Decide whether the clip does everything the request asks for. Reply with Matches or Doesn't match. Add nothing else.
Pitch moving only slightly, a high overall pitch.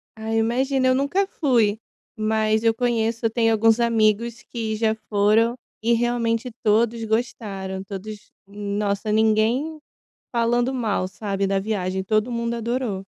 Matches